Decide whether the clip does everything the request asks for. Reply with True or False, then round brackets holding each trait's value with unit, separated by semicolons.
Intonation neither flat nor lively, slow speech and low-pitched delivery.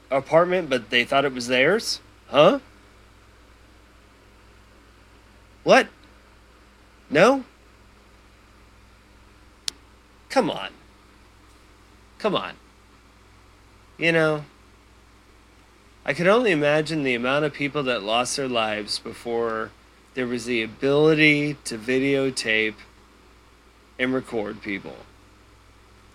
True (4.0 semitones; 85 wpm; 105 Hz)